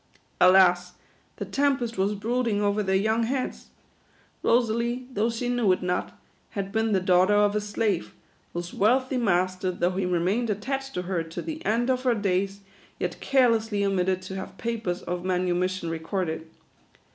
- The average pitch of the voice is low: No, high, 200 Hz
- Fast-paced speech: No, average, 165 wpm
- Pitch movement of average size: Yes, average, 4.1 semitones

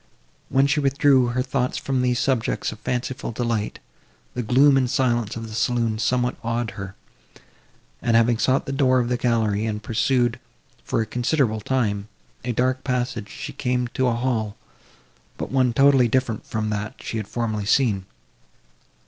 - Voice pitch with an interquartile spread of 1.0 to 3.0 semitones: Yes, average, 2.7 semitones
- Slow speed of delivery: No, average, 165 wpm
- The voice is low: Yes, low, 120 Hz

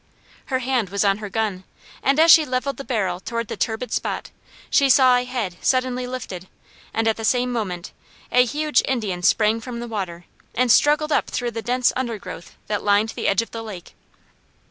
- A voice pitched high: Yes, high, 230 Hz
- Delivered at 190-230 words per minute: Yes, average, 195 wpm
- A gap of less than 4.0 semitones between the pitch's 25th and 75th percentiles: Yes, average, 3.6 semitones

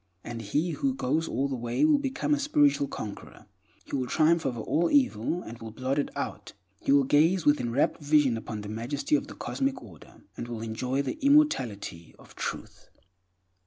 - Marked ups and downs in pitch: Yes, wide, 7.1 semitones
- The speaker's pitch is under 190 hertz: Yes, medium, 140 Hz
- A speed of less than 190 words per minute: No, average, 195 wpm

